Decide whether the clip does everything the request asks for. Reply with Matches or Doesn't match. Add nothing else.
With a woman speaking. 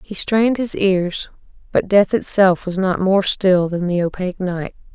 Matches